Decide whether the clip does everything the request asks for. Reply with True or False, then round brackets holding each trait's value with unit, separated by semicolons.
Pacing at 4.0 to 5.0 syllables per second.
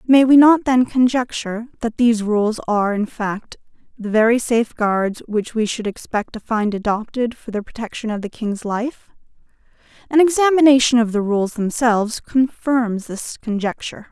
True (4.9 syllables/s)